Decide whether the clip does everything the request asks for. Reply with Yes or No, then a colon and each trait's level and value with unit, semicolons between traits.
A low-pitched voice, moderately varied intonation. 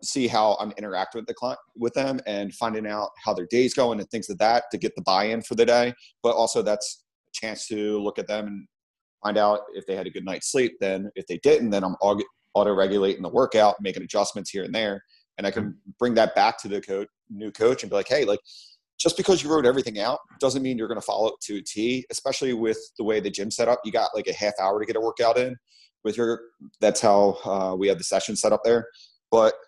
Yes: low, 115 Hz; average, 3.9 semitones